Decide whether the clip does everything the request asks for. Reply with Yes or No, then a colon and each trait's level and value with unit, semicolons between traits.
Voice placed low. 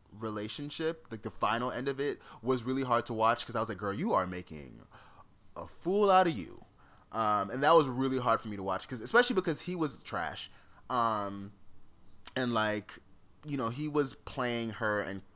Yes: low, 115 Hz